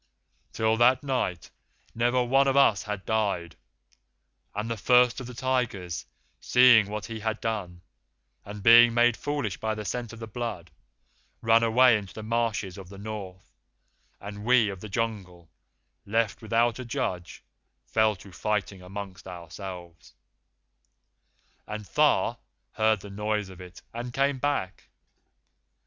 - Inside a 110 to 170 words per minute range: Yes, average, 145 wpm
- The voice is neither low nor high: No, low, 110 Hz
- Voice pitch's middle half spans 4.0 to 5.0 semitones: No, average, 3.4 semitones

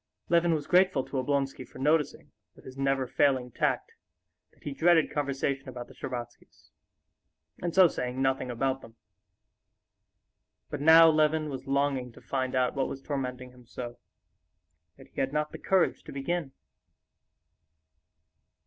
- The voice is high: No, low, 135 Hz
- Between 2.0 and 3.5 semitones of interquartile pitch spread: Yes, average, 2.9 semitones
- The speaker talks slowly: No, average, 150 wpm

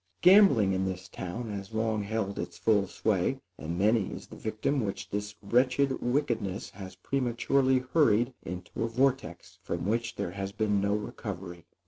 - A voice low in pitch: Yes, low, 110 Hz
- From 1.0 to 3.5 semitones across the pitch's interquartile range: No, average, 3.9 semitones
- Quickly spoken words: No, average, 160 wpm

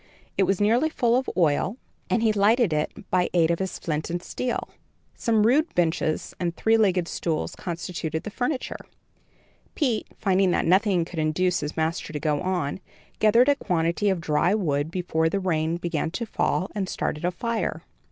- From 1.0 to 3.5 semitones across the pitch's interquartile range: No, average, 4.8 semitones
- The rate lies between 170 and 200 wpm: Yes, average, 180 wpm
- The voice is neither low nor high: Yes, medium, 180 Hz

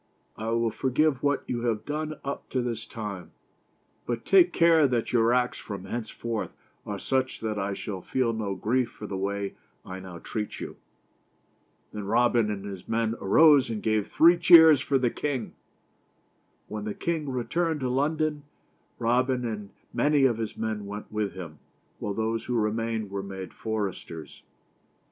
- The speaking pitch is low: Yes, low, 115 Hz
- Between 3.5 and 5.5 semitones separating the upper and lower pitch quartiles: Yes, average, 4.3 semitones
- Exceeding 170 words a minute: No, average, 165 wpm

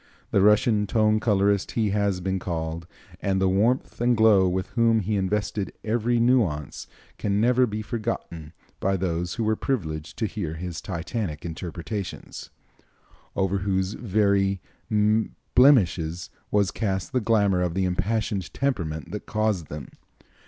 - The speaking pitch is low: Yes, low, 100 Hz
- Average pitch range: Yes, average, 3.5 semitones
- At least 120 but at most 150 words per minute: Yes, average, 140 wpm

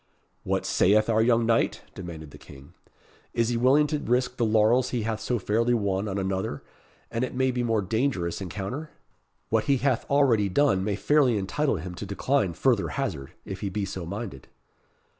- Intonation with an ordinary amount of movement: Yes, average, 4.6 semitones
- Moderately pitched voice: No, low, 110 Hz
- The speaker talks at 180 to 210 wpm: Yes, average, 185 wpm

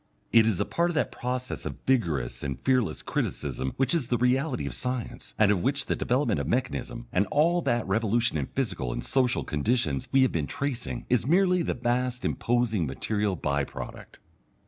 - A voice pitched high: No, low, 120 Hz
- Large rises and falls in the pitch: Yes, wide, 6.3 semitones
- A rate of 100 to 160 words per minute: No, average, 190 wpm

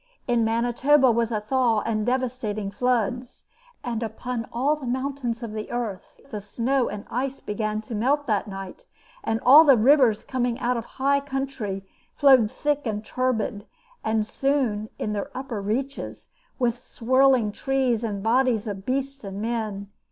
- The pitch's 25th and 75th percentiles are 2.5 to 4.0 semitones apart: Yes, average, 3.6 semitones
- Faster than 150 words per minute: Yes, average, 160 wpm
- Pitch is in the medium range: No, high, 240 Hz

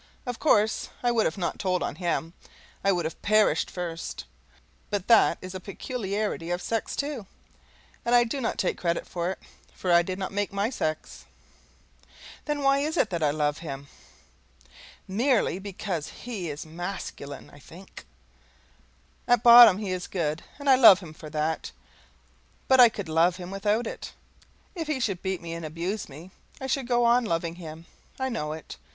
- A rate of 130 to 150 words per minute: No, average, 180 wpm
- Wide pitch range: Yes, wide, 5.7 semitones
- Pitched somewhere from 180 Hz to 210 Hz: Yes, high, 190 Hz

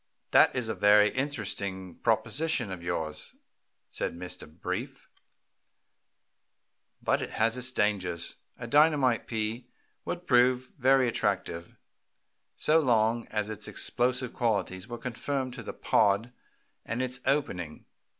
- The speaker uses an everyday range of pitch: Yes, average, 4.3 semitones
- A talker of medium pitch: No, low, 115 Hz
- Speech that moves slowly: Yes, slow, 120 wpm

